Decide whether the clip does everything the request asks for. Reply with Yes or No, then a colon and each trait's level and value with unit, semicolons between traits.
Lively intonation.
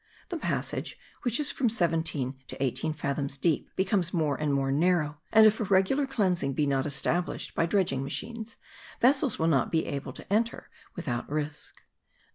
Yes: wide, 7.3 semitones